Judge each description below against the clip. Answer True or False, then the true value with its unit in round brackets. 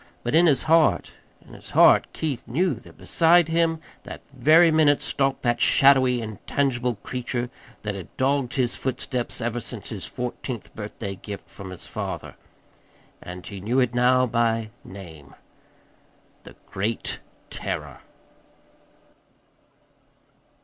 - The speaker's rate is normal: False (130 wpm)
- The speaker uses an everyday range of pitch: True (4.3 semitones)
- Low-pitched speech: True (125 Hz)